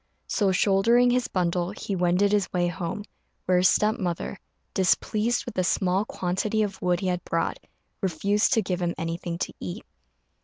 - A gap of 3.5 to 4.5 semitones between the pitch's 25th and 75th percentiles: No, average, 2.8 semitones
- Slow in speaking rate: No, average, 170 wpm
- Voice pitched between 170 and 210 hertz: Yes, medium, 185 Hz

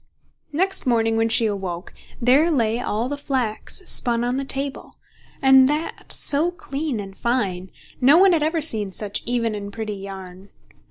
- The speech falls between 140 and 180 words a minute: Yes, average, 165 wpm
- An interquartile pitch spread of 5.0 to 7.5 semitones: Yes, average, 5.3 semitones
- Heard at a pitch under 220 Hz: No, high, 240 Hz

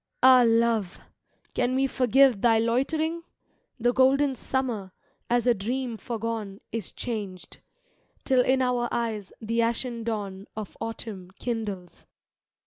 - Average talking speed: No, slow, 125 wpm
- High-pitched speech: Yes, high, 230 Hz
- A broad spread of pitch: No, average, 3.1 semitones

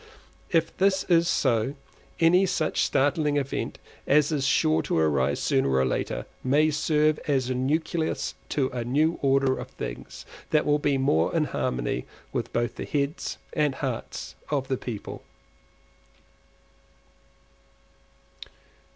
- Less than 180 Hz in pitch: Yes, medium, 140 Hz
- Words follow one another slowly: Yes, slow, 130 wpm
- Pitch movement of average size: Yes, average, 3.3 semitones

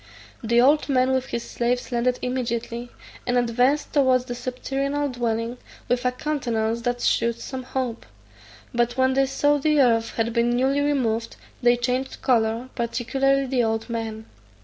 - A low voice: No, high, 245 Hz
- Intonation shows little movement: Yes, narrow, 2.0 semitones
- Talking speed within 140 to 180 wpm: Yes, average, 155 wpm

